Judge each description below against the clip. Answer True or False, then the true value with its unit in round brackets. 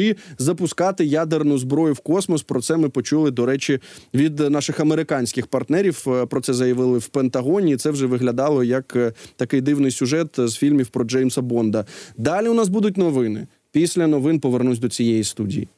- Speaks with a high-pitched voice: False (135 Hz)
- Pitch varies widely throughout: False (3.7 semitones)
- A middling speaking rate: False (165 wpm)